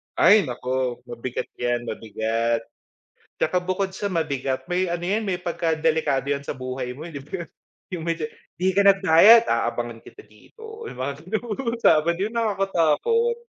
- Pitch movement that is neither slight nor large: No, wide, 7.3 semitones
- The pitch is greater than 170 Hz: No, medium, 160 Hz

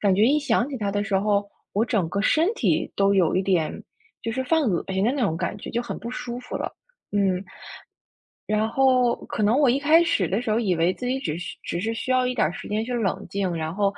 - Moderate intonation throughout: Yes, average, 4.4 semitones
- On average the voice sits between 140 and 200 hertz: No, high, 215 Hz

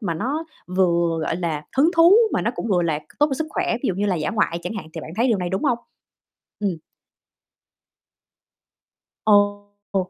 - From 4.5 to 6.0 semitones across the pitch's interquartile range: Yes, average, 5.1 semitones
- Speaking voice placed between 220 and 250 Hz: No, high, 195 Hz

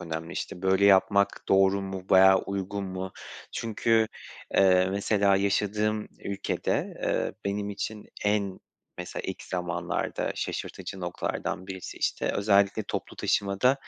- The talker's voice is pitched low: Yes, low, 100 Hz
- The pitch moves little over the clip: Yes, narrow, 1.3 semitones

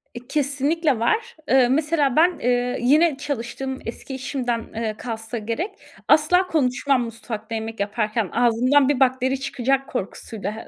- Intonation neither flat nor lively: Yes, average, 3.7 semitones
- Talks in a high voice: Yes, very high, 255 Hz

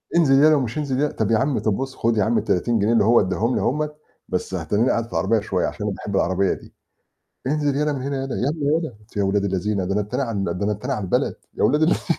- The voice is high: No, low, 115 Hz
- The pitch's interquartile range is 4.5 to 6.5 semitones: Yes, wide, 5.4 semitones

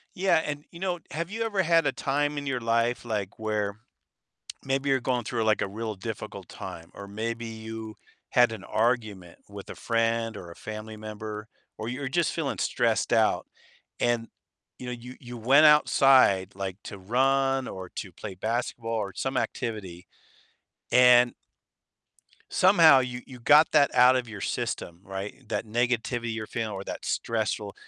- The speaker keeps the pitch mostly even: No, average, 3.7 semitones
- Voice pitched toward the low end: Yes, low, 115 Hz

